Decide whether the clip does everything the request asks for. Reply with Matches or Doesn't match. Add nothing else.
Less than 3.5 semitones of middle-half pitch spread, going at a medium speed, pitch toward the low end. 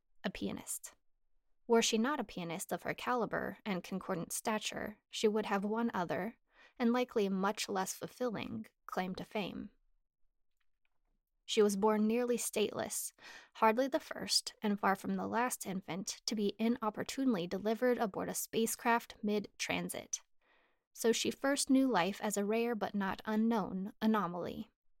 Doesn't match